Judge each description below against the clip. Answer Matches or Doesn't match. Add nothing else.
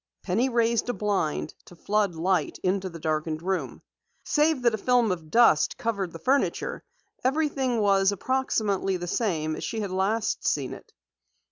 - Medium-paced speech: Matches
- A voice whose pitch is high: Matches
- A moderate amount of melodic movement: Matches